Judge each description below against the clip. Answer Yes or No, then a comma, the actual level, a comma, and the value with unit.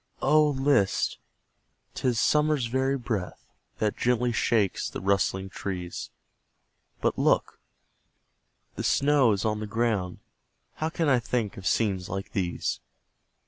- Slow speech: Yes, slow, 125 wpm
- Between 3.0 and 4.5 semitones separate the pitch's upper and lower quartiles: No, average, 5.3 semitones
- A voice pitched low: Yes, low, 115 Hz